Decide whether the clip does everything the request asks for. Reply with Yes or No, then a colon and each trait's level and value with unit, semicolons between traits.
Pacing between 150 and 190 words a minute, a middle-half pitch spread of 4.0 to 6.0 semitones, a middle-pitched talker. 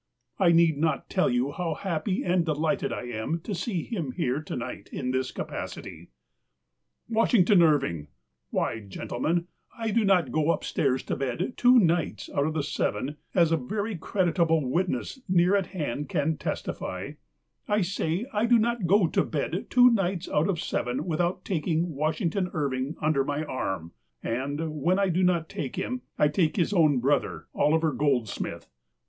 Yes: average, 175 wpm; average, 4.6 semitones; medium, 160 Hz